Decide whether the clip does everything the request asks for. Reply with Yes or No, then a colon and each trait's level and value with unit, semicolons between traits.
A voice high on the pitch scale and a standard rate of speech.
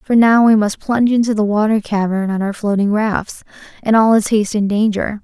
No: high, 215 Hz; fast, 220 wpm